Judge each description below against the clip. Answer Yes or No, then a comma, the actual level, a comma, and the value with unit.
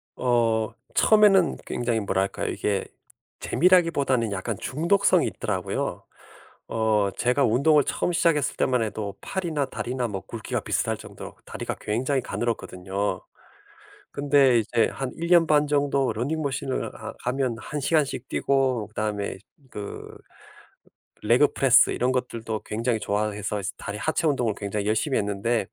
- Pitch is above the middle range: No, low, 125 Hz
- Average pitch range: Yes, average, 5.0 semitones